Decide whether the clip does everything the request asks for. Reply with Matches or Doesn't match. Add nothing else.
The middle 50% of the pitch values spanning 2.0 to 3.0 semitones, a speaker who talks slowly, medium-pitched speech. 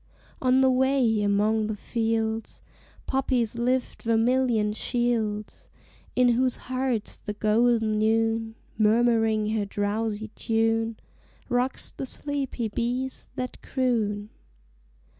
Doesn't match